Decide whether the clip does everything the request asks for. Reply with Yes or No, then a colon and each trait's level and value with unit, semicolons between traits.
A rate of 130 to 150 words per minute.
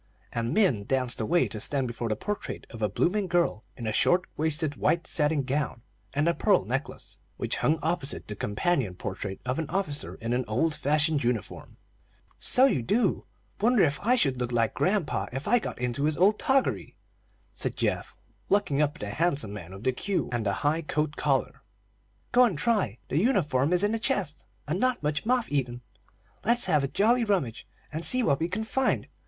No: average, 195 wpm